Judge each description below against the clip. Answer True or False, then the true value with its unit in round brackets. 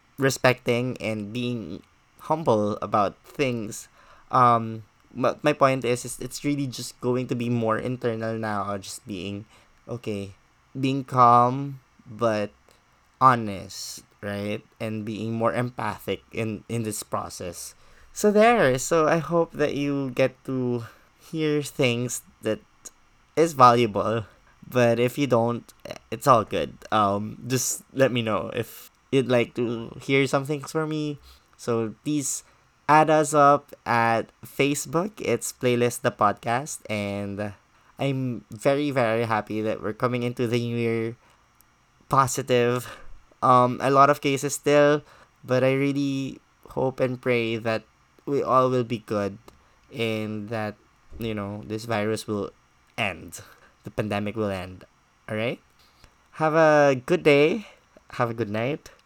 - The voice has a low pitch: True (120 Hz)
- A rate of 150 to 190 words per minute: False (135 wpm)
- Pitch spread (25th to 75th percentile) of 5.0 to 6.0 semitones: False (3.8 semitones)